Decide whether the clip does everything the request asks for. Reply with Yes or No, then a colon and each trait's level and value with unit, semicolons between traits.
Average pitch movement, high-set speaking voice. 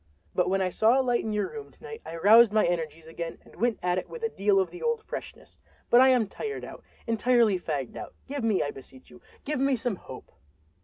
No: wide, 6.4 semitones; high, 220 Hz